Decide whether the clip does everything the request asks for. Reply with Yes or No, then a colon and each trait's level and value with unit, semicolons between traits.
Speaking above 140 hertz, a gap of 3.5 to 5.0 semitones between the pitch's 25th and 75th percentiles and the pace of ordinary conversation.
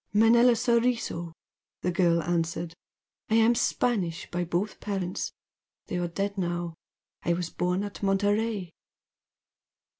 No: medium, 185 Hz; average, 4.1 semitones; slow, 120 wpm